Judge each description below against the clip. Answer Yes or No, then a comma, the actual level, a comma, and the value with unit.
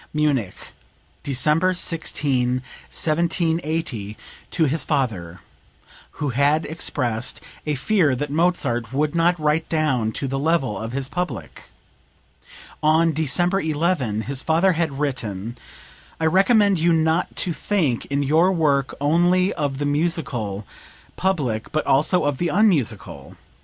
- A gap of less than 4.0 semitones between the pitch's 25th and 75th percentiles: No, average, 4.4 semitones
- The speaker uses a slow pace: Yes, slow, 125 wpm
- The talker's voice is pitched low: No, medium, 150 Hz